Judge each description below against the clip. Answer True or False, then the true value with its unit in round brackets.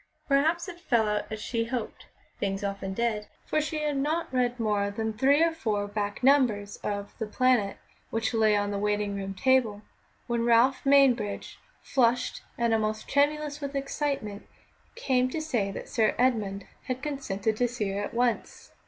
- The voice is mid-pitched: False (235 Hz)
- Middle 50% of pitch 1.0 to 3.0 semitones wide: False (4.8 semitones)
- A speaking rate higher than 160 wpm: True (170 wpm)